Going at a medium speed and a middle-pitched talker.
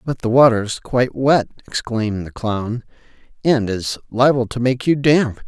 No: average, 175 wpm; low, 120 Hz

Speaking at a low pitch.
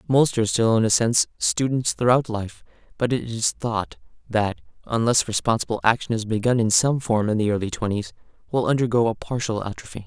Yes: low, 115 Hz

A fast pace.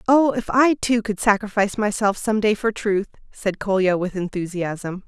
No: average, 175 wpm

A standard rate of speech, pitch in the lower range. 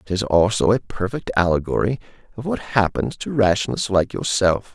Yes: average, 165 wpm; low, 105 Hz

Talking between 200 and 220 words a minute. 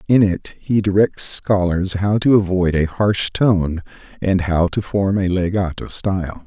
No: average, 165 wpm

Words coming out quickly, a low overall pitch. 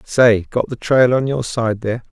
Yes: fast, 220 wpm; low, 120 Hz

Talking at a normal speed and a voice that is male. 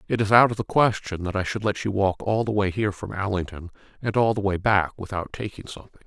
No: fast, 255 wpm; male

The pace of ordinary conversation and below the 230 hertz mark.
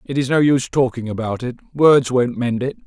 No: fast, 230 wpm; low, 130 Hz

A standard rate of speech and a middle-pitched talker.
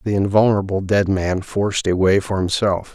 No: average, 185 wpm; low, 100 Hz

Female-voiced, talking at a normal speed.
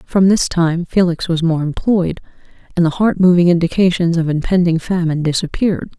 Yes: female; average, 160 wpm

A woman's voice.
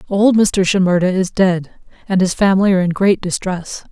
Yes: female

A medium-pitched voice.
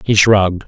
No: low, 100 Hz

